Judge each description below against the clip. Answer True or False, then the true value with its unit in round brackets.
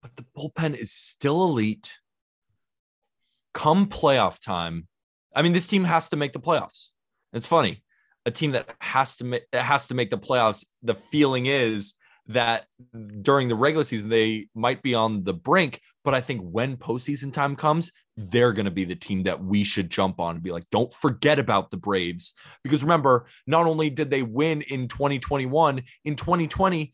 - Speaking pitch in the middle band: False (130 Hz)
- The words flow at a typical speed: True (185 wpm)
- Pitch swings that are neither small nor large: False (5.8 semitones)